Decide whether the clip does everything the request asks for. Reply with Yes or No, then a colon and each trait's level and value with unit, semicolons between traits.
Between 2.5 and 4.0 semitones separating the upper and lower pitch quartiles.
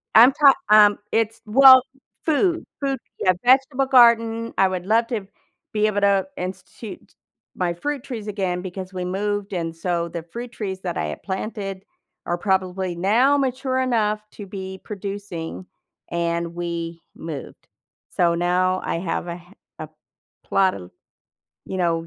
No: average, 4.4 semitones